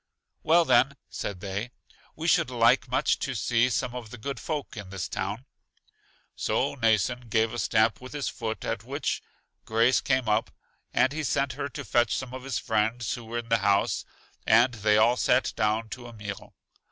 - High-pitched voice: No, low, 115 Hz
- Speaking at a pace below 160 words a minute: No, average, 190 wpm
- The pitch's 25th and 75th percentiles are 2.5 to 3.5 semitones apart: Yes, average, 2.9 semitones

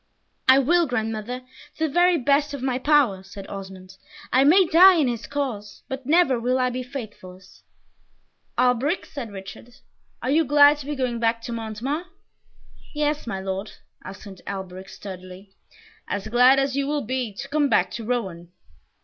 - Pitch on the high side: Yes, very high, 250 Hz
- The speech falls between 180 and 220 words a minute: No, average, 165 wpm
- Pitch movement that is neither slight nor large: No, wide, 5.8 semitones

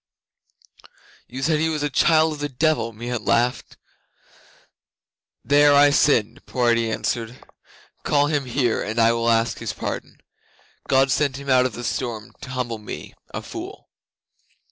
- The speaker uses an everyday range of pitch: Yes, average, 3.7 semitones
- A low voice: Yes, low, 130 Hz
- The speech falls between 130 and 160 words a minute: Yes, average, 155 wpm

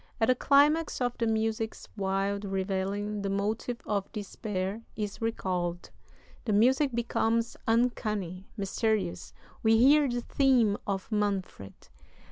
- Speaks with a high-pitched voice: Yes, high, 215 Hz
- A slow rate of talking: Yes, slow, 120 wpm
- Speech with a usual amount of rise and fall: Yes, average, 3.1 semitones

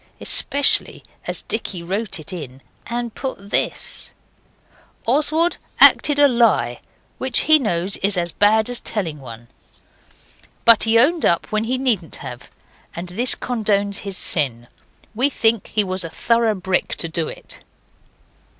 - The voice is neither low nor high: No, high, 210 Hz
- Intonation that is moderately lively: No, wide, 5.8 semitones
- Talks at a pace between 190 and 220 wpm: No, average, 145 wpm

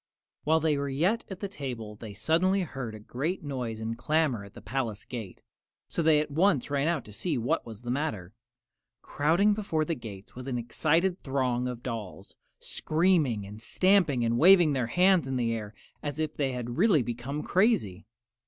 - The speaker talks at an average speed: Yes, average, 190 wpm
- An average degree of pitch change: No, wide, 5.8 semitones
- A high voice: No, low, 135 Hz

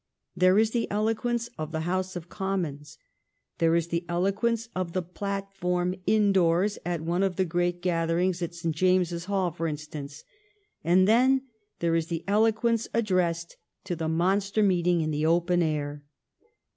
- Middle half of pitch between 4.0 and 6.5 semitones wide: No, average, 2.9 semitones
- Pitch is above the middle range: No, medium, 180 Hz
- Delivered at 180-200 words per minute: No, average, 160 wpm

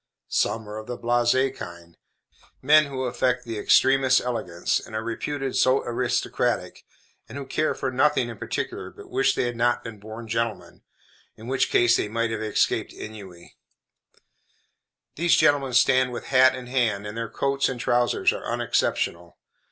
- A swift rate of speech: No, average, 165 wpm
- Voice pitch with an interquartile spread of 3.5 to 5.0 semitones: No, average, 3.0 semitones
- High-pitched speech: No, low, 120 Hz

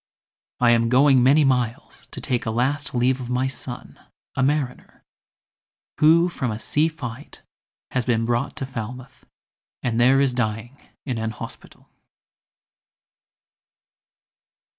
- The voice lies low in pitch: Yes, low, 125 Hz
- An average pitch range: No, narrow, 2.3 semitones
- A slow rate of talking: Yes, slow, 130 wpm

